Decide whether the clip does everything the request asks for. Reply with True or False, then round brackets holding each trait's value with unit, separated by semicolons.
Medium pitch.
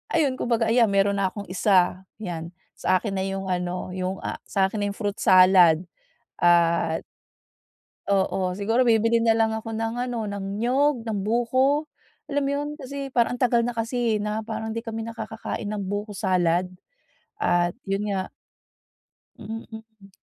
False (215 Hz)